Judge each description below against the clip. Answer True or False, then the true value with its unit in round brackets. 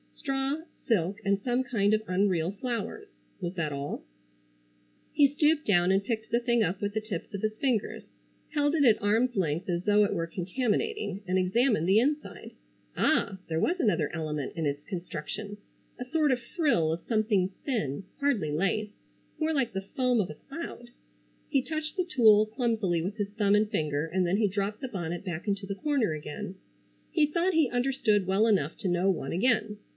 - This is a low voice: False (210 Hz)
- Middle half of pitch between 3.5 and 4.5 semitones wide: False (5.4 semitones)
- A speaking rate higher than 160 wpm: True (185 wpm)